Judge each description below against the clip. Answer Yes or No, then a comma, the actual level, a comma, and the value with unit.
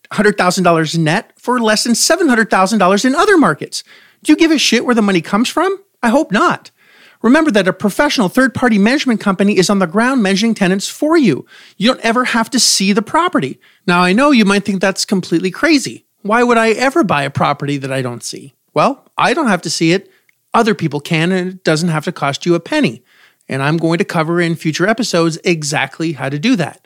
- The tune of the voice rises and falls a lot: Yes, wide, 6.3 semitones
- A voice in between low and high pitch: No, high, 205 Hz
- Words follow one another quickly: Yes, fast, 220 wpm